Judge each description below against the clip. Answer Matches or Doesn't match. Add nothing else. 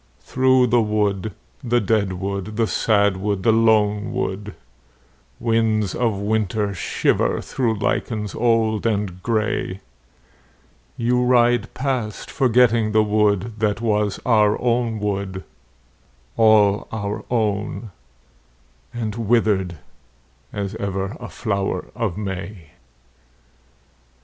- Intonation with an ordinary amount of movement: Doesn't match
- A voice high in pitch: Doesn't match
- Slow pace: Matches